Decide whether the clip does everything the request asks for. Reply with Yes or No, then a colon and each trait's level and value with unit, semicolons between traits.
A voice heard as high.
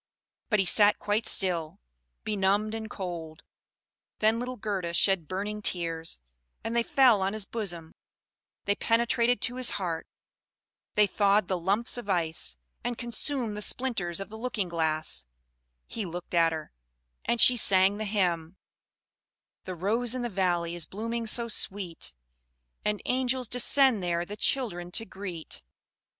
Yes: high, 205 Hz